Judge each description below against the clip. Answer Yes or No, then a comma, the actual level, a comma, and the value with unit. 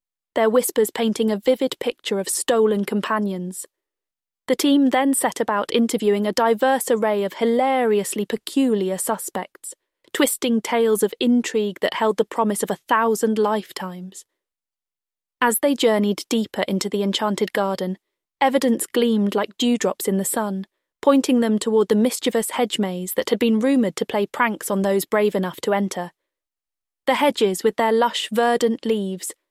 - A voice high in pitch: Yes, high, 225 Hz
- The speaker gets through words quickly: No, average, 155 wpm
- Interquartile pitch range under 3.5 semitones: Yes, average, 3.0 semitones